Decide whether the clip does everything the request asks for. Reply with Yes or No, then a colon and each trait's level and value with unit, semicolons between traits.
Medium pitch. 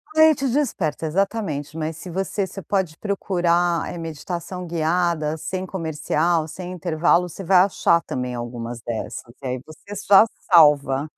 Yes: medium, 170 Hz